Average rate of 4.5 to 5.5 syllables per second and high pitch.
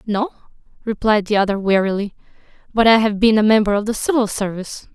No: 6.3 syllables/s; high, 215 Hz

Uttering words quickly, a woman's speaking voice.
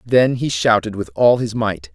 No: fast, 215 wpm; male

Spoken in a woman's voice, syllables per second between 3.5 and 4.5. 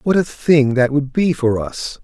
No: male; 4.2 syllables/s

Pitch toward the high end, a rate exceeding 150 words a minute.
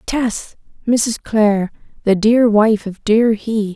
No: high, 220 Hz; slow, 110 wpm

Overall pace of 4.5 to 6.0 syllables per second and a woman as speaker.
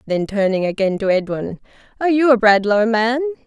Yes: 5.6 syllables/s; female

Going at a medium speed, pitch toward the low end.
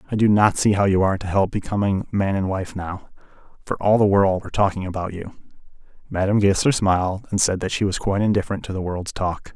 No: fast, 225 wpm; very low, 95 Hz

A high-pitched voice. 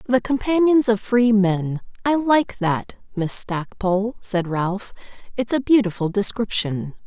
Yes: high, 215 Hz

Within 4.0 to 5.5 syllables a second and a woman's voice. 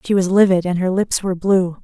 No: 5.9 syllables/s; female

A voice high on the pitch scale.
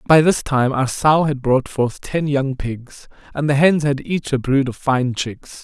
No: medium, 140 Hz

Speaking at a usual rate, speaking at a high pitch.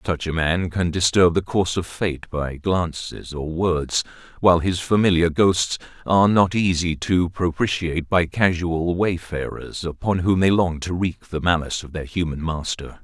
No: average, 170 wpm; very low, 85 Hz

